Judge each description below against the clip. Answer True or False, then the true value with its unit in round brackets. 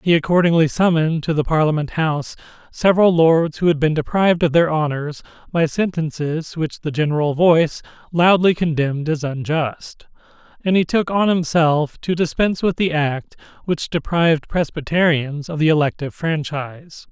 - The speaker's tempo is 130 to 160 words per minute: True (150 wpm)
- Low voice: False (160 Hz)